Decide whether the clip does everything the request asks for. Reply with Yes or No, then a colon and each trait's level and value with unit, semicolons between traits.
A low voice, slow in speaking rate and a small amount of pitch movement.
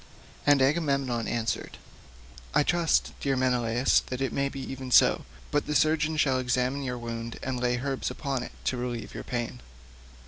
No: low, 130 Hz; average, 170 wpm; narrow, 2.1 semitones